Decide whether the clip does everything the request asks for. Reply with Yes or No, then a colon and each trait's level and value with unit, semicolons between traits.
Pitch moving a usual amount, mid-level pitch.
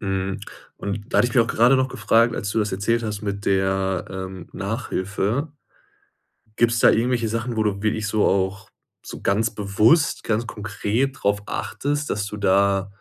No: average, 3.0 semitones; low, 105 Hz